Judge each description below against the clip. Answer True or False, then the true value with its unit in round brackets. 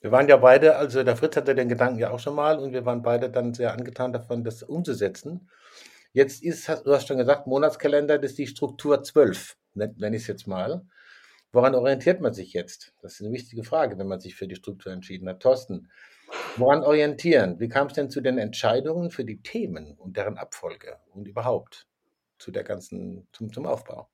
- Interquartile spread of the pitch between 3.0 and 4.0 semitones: True (3.4 semitones)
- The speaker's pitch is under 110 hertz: False (135 Hz)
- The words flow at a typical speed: False (205 wpm)